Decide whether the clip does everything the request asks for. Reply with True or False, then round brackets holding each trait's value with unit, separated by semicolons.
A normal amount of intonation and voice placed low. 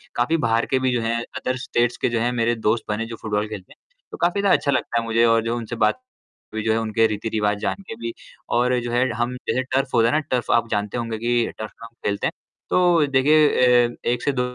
False (2.2 semitones; 120 Hz)